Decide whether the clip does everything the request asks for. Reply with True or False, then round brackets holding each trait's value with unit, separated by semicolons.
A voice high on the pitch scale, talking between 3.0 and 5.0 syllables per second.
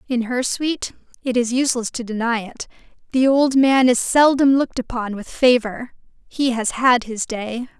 True (245 Hz; 4.8 syllables/s)